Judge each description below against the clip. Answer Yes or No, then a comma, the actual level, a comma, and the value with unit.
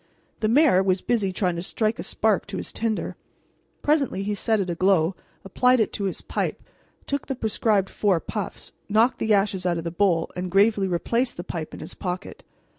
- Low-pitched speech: No, high, 200 Hz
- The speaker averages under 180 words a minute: No, average, 195 wpm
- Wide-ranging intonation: No, average, 3.3 semitones